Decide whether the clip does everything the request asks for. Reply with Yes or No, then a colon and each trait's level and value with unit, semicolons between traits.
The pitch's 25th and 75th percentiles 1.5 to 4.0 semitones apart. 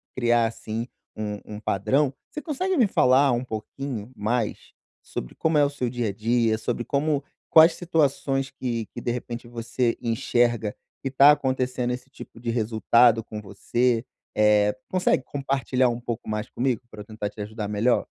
Yes: average, 3.4 semitones